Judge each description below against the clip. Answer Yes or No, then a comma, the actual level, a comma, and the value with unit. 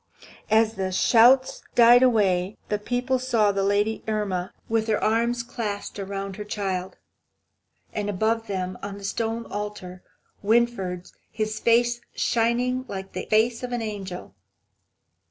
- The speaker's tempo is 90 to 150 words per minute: Yes, slow, 135 wpm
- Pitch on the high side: Yes, high, 215 Hz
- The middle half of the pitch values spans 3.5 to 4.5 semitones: No, average, 2.9 semitones